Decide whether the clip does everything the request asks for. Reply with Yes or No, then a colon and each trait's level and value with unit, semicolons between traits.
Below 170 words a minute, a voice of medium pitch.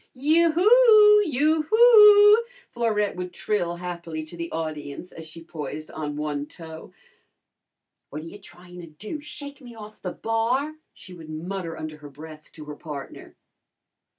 Yes: average, 155 wpm; medium, 180 Hz